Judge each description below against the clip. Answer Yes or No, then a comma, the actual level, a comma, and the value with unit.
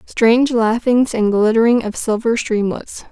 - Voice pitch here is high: Yes, high, 230 Hz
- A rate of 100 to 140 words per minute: Yes, slow, 135 wpm